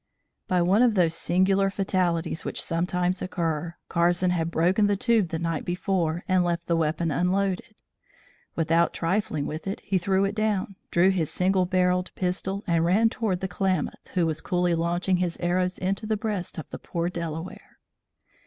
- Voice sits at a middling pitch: Yes, medium, 180 Hz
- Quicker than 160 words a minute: Yes, average, 170 wpm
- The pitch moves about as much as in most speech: No, narrow, 2.3 semitones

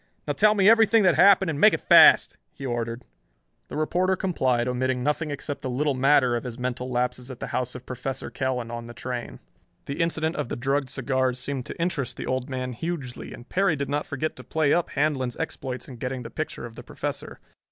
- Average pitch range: Yes, average, 3.7 semitones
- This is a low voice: Yes, low, 130 Hz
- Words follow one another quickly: Yes, fast, 225 wpm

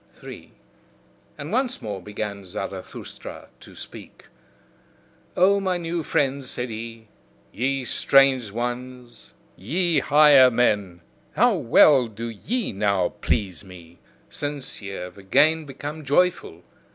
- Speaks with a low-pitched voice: Yes, low, 125 Hz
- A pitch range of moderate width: No, wide, 6.4 semitones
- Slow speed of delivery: Yes, slow, 115 wpm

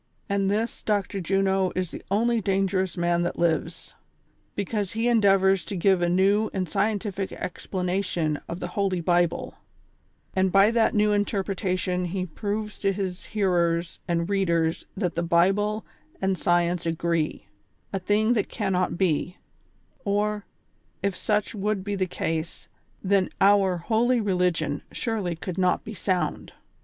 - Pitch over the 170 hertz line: Yes, high, 190 Hz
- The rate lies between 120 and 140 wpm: No, average, 150 wpm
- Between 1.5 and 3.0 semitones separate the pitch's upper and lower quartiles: Yes, narrow, 2.6 semitones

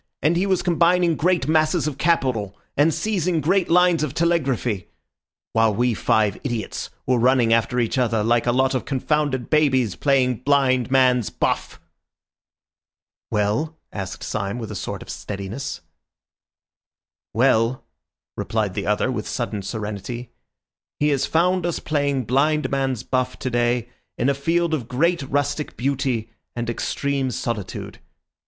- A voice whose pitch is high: No, low, 130 Hz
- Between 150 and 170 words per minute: No, average, 140 wpm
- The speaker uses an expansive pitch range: No, average, 4.9 semitones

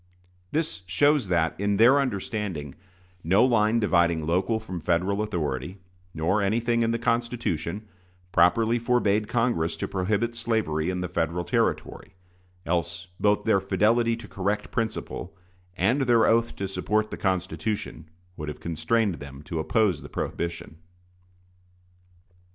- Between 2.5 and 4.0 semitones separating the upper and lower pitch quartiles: No, average, 5.1 semitones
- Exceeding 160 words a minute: No, slow, 135 wpm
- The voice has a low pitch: Yes, low, 100 Hz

